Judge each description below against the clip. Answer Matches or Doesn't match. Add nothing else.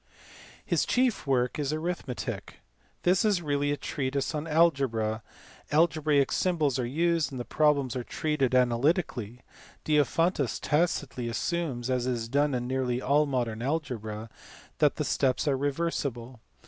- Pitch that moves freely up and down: Doesn't match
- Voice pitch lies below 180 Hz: Matches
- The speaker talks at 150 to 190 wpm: Doesn't match